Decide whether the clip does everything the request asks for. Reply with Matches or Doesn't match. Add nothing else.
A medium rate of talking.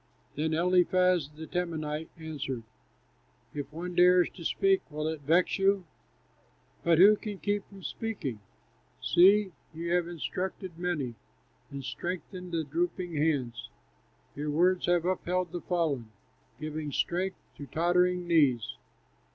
Doesn't match